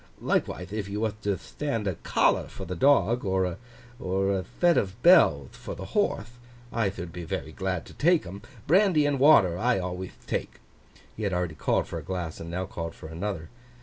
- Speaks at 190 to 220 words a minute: Yes, average, 195 wpm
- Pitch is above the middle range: No, low, 100 Hz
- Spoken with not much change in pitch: No, average, 5.2 semitones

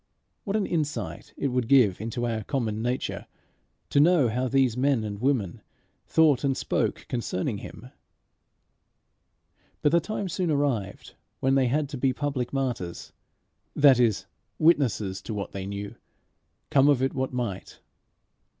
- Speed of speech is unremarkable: Yes, average, 150 wpm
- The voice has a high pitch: No, low, 130 Hz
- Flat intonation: No, average, 4.5 semitones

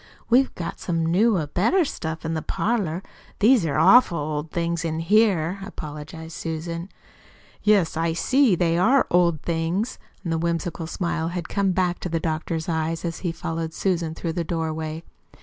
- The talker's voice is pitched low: No, medium, 170 Hz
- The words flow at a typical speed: Yes, average, 165 wpm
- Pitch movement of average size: No, narrow, 2.3 semitones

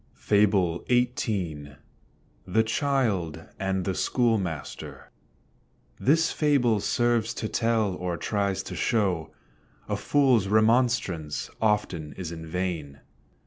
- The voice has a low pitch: Yes, low, 100 Hz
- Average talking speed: No, slow, 100 wpm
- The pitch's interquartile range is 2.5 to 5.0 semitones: No, wide, 5.4 semitones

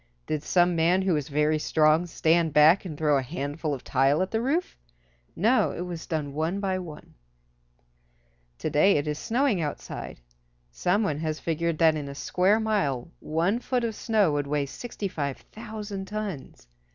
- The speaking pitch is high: No, medium, 165 Hz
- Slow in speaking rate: No, average, 170 wpm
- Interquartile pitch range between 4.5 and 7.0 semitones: Yes, average, 4.9 semitones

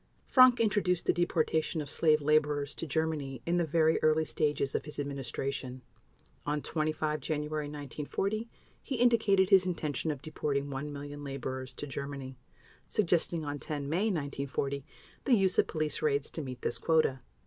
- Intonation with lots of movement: No, average, 2.9 semitones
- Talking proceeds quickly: No, average, 160 wpm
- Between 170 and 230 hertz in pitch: No, medium, 150 Hz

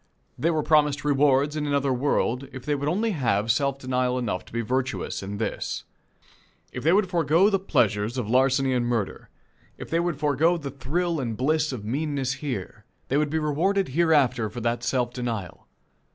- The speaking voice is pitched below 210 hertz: Yes, low, 135 Hz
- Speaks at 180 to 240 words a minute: Yes, average, 185 wpm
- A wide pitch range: No, average, 3.8 semitones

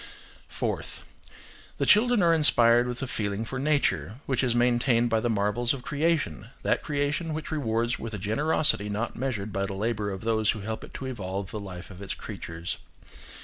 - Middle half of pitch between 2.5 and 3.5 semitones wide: No, average, 5.0 semitones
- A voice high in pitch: No, low, 115 Hz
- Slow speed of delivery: No, average, 185 wpm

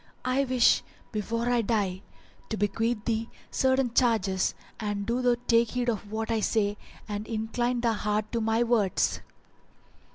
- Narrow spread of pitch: Yes, narrow, 2.3 semitones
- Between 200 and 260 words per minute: No, average, 155 wpm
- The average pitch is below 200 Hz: No, high, 225 Hz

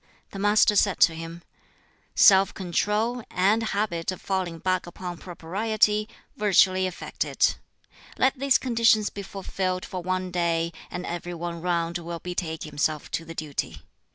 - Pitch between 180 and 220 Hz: Yes, medium, 185 Hz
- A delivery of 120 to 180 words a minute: Yes, average, 155 wpm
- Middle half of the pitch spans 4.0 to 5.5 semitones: No, average, 3.4 semitones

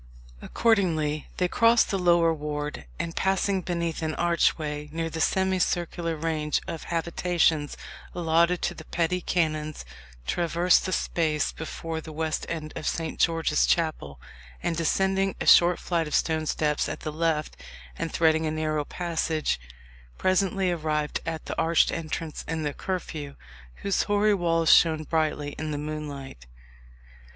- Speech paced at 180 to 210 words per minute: No, average, 145 wpm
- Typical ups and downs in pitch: No, narrow, 2.1 semitones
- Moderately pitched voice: Yes, medium, 165 Hz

